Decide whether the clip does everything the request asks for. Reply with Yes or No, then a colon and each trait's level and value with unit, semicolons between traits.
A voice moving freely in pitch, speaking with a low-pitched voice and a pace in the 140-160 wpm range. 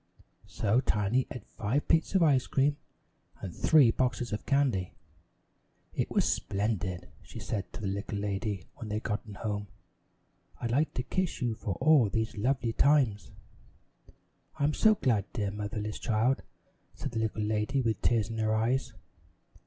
No: average, 4.1 semitones; low, 110 Hz; average, 155 wpm